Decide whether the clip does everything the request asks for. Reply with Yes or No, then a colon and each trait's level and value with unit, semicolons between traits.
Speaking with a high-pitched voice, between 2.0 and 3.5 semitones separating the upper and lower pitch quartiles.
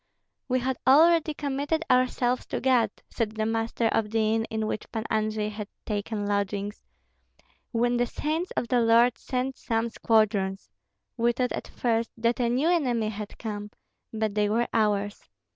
Yes: high, 230 Hz; average, 2.7 semitones